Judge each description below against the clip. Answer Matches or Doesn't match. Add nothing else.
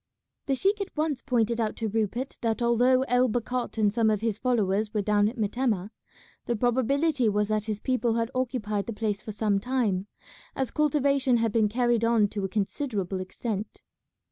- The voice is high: Matches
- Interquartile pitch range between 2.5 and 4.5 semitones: Matches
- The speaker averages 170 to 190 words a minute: Matches